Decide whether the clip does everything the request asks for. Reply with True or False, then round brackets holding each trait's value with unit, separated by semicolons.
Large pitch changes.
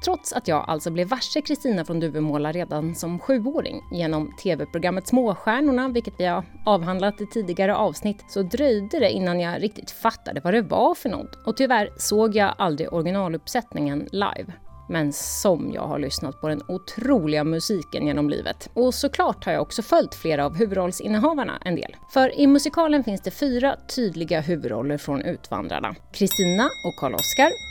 True (7.1 semitones)